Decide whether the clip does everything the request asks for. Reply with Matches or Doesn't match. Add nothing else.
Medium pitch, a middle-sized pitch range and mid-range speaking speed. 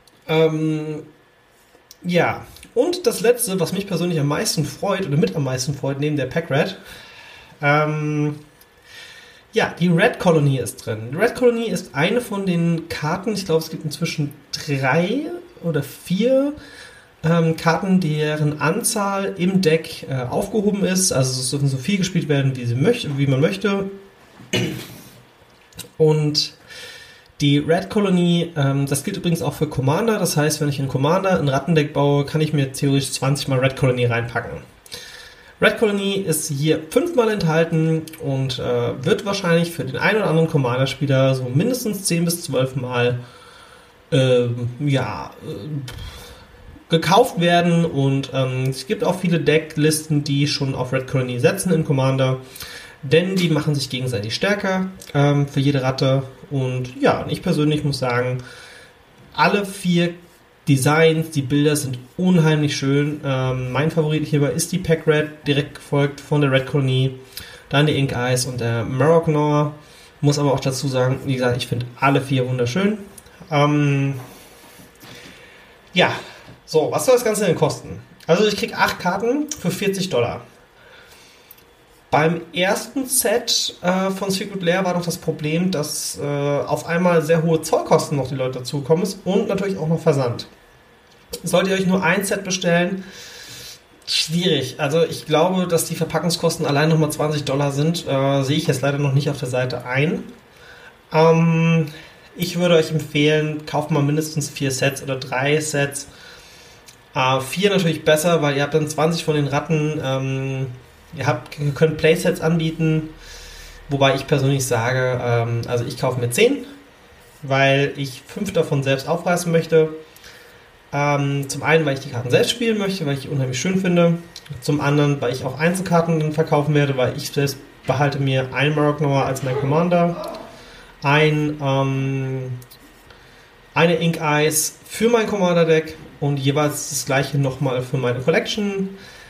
Matches